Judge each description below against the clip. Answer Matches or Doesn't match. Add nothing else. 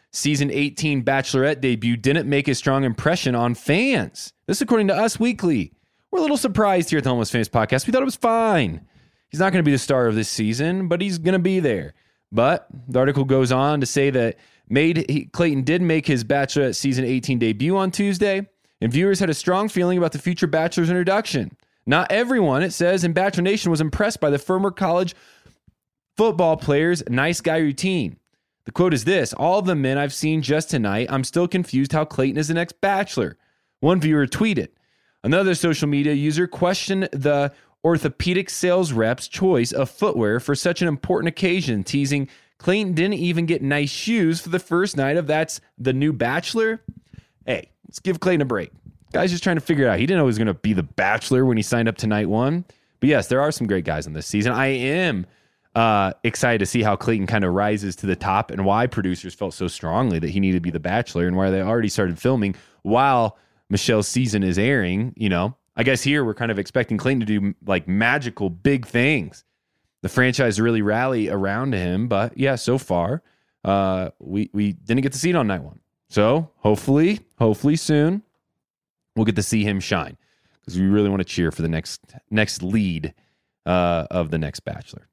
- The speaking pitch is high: Doesn't match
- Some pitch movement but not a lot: Doesn't match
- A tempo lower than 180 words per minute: Doesn't match